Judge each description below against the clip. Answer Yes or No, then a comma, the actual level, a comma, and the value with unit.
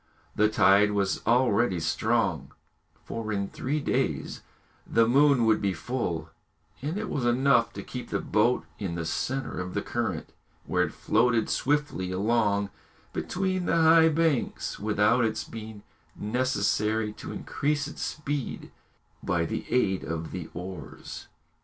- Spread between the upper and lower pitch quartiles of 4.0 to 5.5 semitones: Yes, average, 5.2 semitones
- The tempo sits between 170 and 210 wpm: No, average, 140 wpm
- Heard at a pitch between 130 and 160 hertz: No, low, 115 Hz